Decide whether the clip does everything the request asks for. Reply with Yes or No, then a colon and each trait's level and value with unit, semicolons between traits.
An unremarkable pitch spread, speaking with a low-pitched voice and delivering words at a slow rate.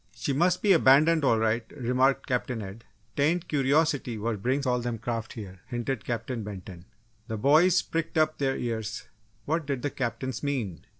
No: average, 4.2 semitones; low, 125 Hz; average, 170 wpm